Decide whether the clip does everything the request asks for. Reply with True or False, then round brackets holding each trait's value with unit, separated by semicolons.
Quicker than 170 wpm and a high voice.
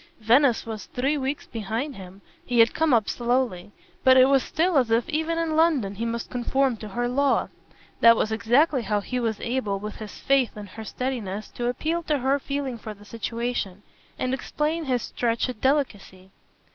True (185 wpm; 245 Hz)